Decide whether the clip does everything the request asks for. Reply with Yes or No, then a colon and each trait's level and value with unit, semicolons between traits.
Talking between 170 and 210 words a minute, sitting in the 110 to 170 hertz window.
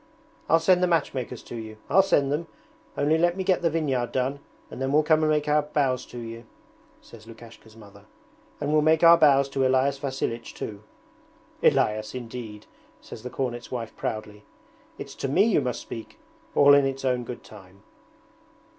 Yes: average, 180 wpm; low, 135 Hz